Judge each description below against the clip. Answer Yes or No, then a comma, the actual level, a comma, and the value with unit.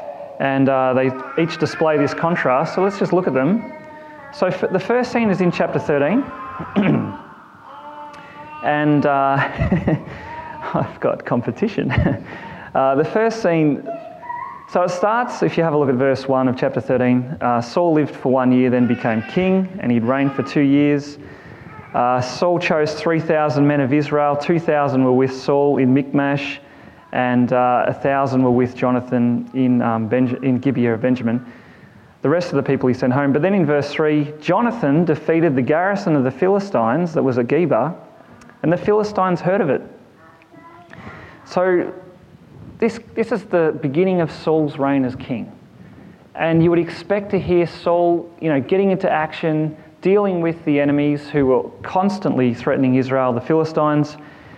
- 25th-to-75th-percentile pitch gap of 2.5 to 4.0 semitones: No, average, 5.3 semitones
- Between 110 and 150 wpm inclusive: No, average, 165 wpm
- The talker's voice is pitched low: No, medium, 150 Hz